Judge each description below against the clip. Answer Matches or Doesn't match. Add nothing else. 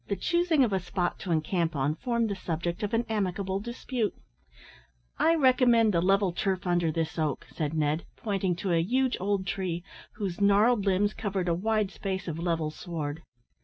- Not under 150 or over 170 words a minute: Doesn't match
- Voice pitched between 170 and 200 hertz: Matches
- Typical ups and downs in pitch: Matches